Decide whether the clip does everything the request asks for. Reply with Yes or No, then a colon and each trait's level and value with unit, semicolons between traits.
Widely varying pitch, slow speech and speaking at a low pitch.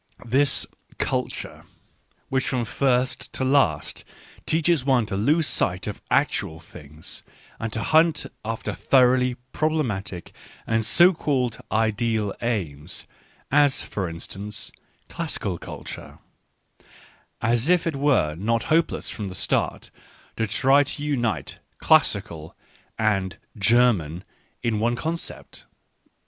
Yes: wide, 5.7 semitones; slow, 130 wpm; low, 115 Hz